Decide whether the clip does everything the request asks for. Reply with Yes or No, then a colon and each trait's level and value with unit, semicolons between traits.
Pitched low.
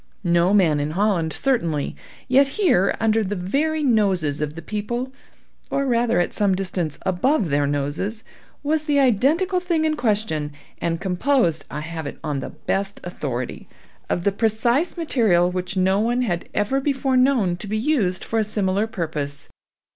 No: high, 205 Hz